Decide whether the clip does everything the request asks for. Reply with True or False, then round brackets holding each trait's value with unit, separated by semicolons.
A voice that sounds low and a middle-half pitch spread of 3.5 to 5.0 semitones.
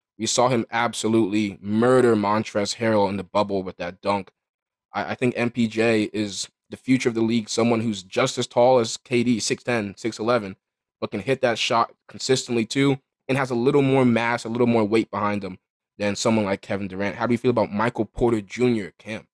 False (115 Hz; 2.8 semitones)